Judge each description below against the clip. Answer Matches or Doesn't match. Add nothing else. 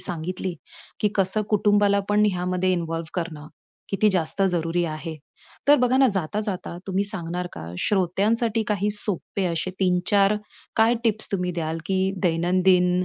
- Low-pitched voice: Doesn't match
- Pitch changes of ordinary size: Matches